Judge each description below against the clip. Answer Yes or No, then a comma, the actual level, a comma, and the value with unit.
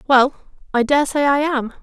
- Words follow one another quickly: No, average, 165 wpm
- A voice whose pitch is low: No, very high, 275 Hz